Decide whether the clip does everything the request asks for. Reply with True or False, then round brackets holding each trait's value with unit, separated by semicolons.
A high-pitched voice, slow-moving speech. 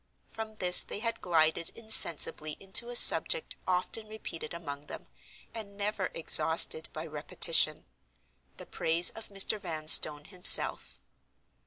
False (180 Hz; 120 wpm)